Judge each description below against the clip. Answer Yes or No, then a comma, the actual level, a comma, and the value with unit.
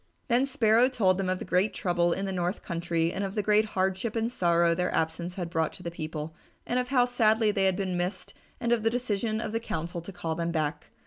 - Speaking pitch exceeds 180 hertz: Yes, high, 190 Hz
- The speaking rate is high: Yes, fast, 245 wpm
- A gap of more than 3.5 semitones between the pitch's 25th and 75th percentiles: Yes, average, 4.4 semitones